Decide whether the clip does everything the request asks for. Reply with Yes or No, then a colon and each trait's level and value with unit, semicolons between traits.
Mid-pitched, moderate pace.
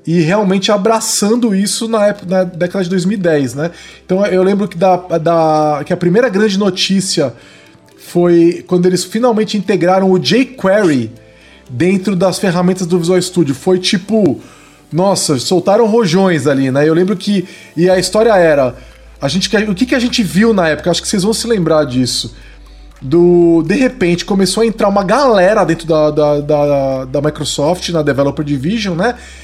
Yes: medium, 180 Hz; average, 170 wpm